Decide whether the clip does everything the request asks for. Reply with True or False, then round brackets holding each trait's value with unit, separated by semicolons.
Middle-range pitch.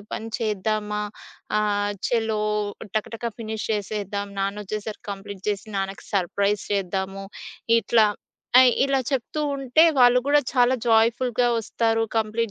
False (215 Hz)